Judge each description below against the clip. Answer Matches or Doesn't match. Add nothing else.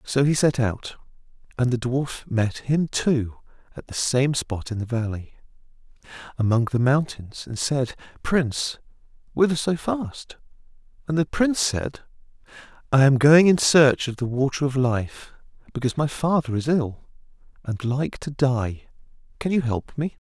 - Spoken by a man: Matches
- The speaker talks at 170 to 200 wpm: Doesn't match